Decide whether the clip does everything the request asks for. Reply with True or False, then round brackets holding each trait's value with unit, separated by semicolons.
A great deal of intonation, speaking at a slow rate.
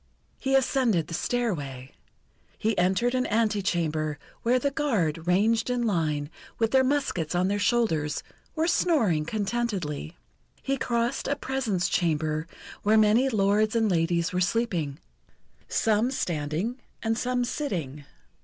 True (6.6 semitones; 130 wpm)